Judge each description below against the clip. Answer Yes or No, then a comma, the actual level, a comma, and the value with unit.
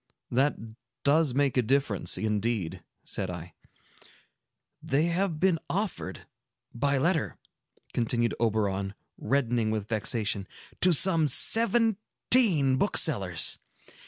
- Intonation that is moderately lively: No, wide, 7.2 semitones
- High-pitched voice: No, low, 130 Hz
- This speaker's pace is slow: Yes, slow, 100 wpm